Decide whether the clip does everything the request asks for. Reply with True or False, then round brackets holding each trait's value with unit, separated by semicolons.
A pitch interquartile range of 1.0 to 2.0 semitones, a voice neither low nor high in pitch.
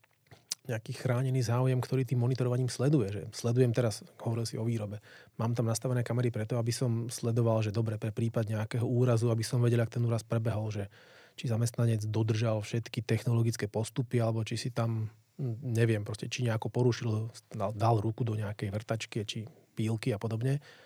False (1.7 semitones; 115 Hz)